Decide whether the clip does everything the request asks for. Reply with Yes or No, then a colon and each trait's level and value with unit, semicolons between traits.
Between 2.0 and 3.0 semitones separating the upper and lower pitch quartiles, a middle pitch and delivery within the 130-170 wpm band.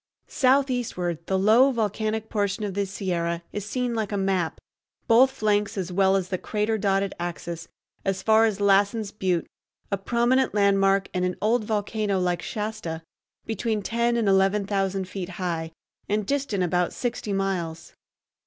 No: average, 2.7 semitones; high, 200 Hz; average, 155 wpm